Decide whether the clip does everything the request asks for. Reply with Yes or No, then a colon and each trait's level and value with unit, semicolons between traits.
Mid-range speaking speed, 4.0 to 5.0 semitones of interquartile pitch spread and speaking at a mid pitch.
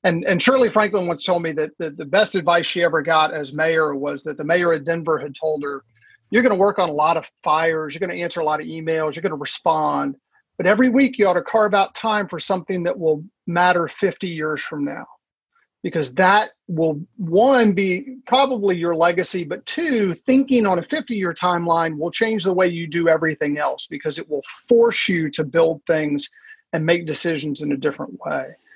No: fast, 215 wpm; average, 4.4 semitones; medium, 175 Hz